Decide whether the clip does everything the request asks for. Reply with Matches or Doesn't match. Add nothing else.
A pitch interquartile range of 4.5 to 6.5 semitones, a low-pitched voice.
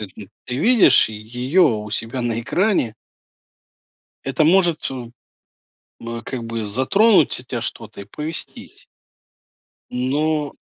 Matches